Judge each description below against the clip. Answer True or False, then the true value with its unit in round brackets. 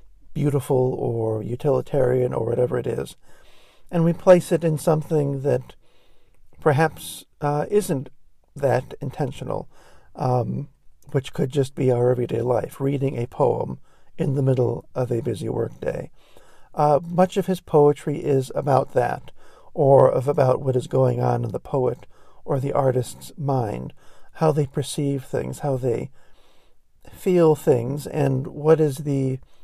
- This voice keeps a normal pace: True (145 wpm)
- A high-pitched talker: False (140 Hz)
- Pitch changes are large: False (3.1 semitones)